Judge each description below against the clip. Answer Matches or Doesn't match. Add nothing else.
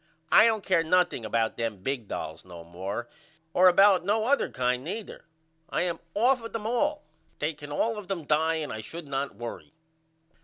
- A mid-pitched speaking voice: Matches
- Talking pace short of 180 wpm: Doesn't match